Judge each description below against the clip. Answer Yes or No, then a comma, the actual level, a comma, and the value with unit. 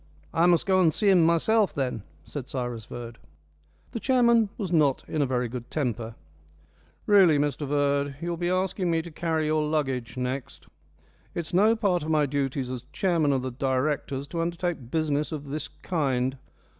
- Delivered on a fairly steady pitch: No, average, 4.6 semitones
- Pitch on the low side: No, medium, 150 Hz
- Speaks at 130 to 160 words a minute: No, average, 175 wpm